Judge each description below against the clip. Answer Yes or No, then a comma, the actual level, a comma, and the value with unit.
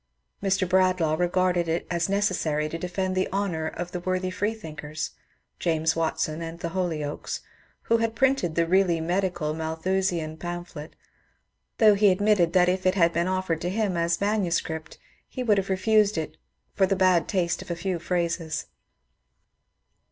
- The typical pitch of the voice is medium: Yes, medium, 180 Hz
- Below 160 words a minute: No, average, 165 wpm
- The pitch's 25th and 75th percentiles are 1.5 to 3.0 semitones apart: Yes, narrow, 2.5 semitones